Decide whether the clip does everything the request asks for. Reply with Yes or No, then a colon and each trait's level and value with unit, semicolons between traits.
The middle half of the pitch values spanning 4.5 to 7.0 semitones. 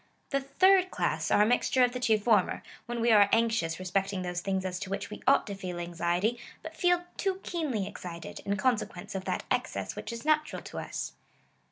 Yes: average, 5.2 semitones